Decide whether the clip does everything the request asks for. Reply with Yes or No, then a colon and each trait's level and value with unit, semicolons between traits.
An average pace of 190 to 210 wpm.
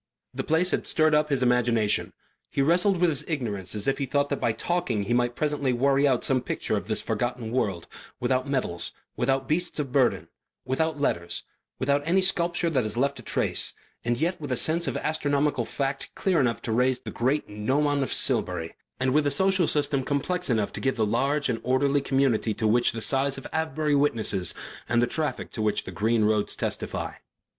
Yes: average, 200 wpm